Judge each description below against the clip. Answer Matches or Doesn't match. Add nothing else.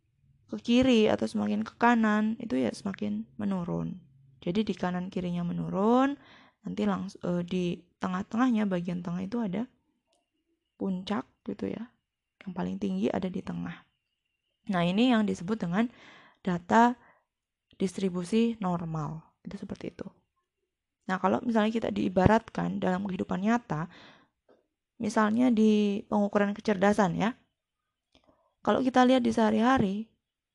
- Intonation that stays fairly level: Doesn't match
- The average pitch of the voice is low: Doesn't match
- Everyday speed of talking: Matches